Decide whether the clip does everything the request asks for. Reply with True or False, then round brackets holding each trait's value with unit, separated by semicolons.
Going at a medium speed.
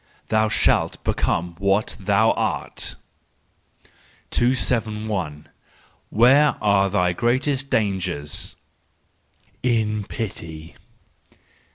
False (70 wpm)